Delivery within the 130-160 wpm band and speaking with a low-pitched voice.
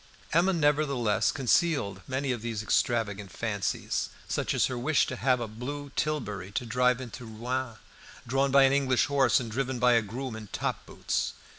No: average, 175 wpm; low, 125 Hz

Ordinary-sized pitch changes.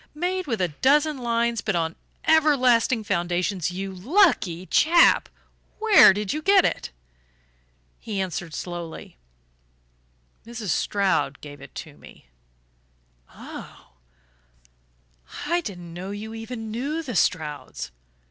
No: wide, 8.1 semitones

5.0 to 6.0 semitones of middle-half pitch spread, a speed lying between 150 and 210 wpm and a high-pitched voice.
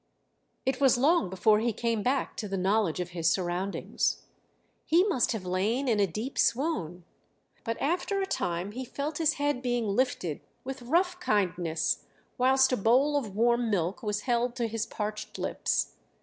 Yes: average, 5.3 semitones; average, 170 wpm; high, 230 Hz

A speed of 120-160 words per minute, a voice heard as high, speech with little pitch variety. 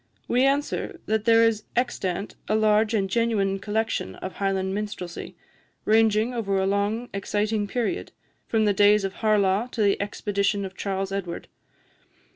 Yes: average, 150 wpm; high, 210 Hz; narrow, 2.2 semitones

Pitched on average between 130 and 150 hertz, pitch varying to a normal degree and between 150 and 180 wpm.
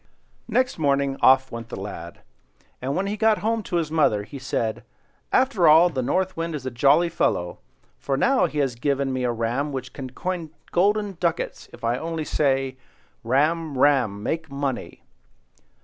Yes: medium, 140 Hz; average, 4.7 semitones; average, 170 wpm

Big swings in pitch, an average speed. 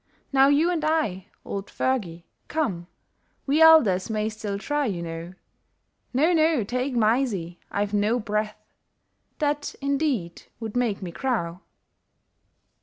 No: wide, 6.4 semitones; slow, 125 wpm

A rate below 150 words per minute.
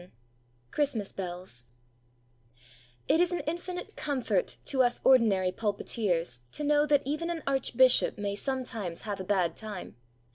Yes: average, 140 wpm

